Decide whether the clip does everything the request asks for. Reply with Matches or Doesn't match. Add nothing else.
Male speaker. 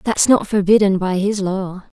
Doesn't match